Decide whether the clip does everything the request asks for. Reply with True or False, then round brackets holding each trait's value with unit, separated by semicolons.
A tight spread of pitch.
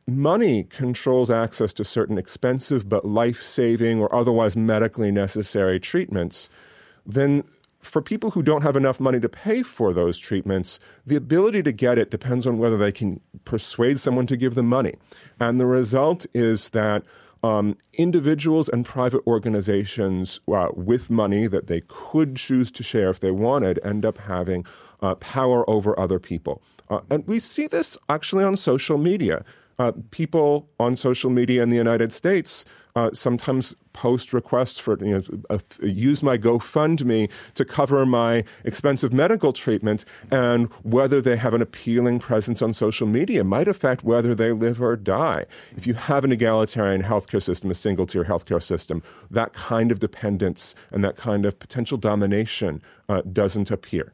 False (4.0 semitones)